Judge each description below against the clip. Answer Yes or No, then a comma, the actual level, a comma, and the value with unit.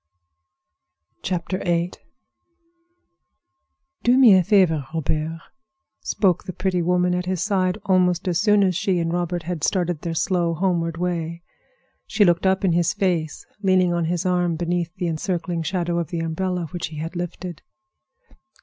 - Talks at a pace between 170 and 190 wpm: No, average, 150 wpm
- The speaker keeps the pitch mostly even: Yes, narrow, 1.7 semitones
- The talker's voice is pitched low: No, medium, 175 Hz